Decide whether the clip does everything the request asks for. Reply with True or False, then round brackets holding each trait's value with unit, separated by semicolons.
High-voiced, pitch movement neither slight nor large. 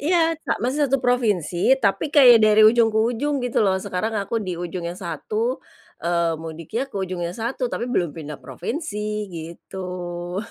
False (210 Hz; 5.8 semitones)